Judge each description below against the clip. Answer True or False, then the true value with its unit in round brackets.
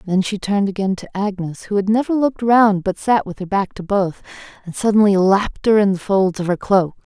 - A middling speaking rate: False (235 wpm)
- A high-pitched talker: True (200 Hz)